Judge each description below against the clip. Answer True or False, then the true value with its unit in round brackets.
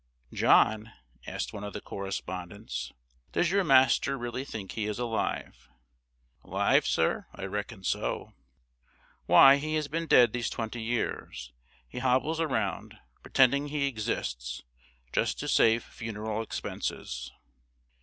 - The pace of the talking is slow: True (125 wpm)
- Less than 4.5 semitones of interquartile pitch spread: False (5.0 semitones)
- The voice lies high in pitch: False (115 Hz)